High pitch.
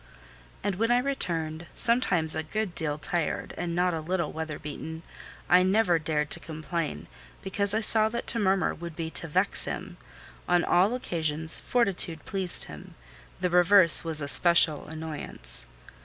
No: medium, 170 Hz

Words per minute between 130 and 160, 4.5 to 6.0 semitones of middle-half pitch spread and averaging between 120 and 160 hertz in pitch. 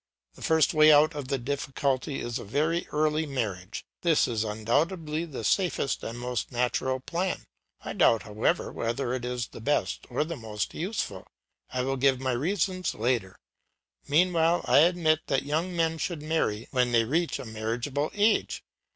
No: average, 170 wpm; average, 5.1 semitones; medium, 140 Hz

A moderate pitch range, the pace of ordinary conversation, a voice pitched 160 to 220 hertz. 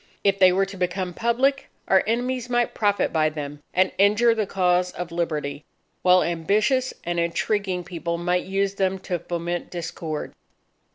Yes: average, 3.1 semitones; average, 160 wpm; medium, 185 Hz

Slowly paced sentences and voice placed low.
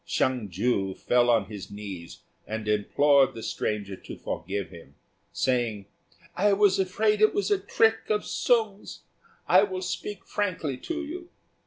No: average, 150 wpm; low, 130 Hz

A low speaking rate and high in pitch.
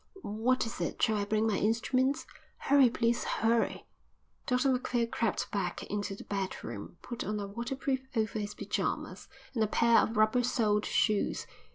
No: average, 165 wpm; high, 225 Hz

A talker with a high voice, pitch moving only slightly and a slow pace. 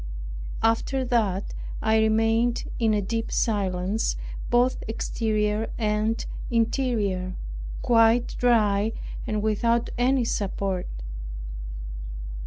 Yes: high, 225 Hz; narrow, 2.0 semitones; slow, 85 wpm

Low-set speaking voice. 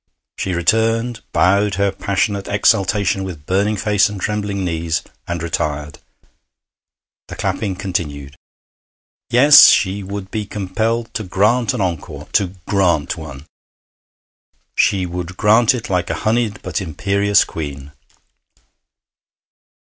Yes: low, 100 Hz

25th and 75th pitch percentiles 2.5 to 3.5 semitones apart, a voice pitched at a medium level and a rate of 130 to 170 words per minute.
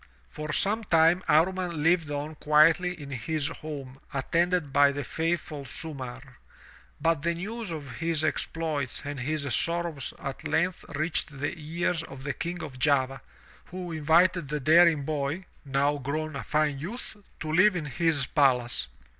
Yes: average, 3.1 semitones; medium, 155 Hz; average, 160 wpm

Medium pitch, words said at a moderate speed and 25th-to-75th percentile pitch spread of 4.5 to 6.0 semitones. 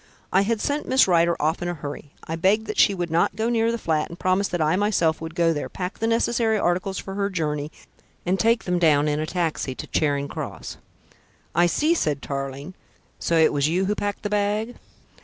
No: medium, 175 Hz; fast, 225 wpm; average, 4.8 semitones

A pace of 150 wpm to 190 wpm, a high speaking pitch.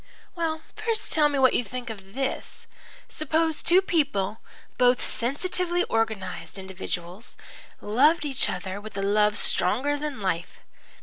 No: slow, 135 wpm; very high, 255 Hz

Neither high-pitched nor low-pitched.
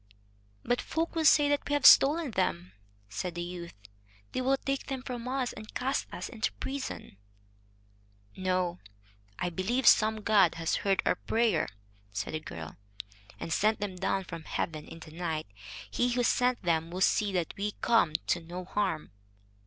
No: high, 195 Hz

